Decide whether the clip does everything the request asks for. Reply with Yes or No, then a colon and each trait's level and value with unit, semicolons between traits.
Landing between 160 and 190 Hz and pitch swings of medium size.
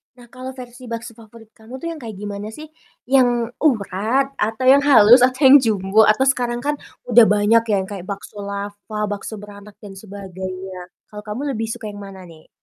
No: high, 220 Hz; average, 3.8 semitones